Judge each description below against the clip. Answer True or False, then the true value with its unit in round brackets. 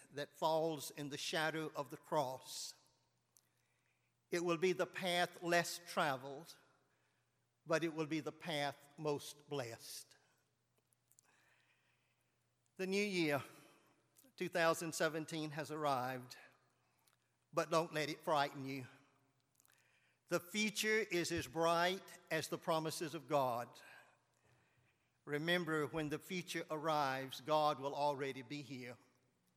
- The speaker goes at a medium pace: False (110 wpm)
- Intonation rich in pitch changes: False (3.3 semitones)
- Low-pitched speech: False (155 Hz)